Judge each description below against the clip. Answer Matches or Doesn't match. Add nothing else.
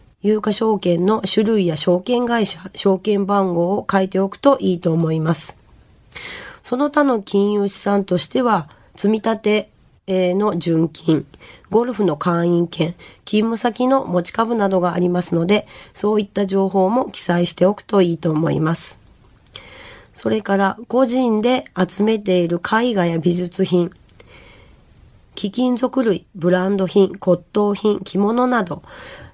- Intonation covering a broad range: Doesn't match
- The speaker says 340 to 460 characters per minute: Doesn't match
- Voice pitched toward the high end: Matches